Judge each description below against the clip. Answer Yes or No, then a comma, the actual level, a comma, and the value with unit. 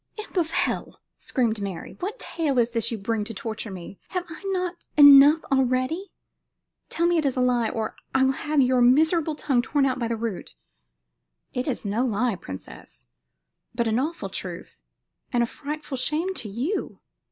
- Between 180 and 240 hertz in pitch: No, very high, 255 Hz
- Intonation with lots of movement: No, average, 5.0 semitones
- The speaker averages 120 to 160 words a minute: No, average, 185 wpm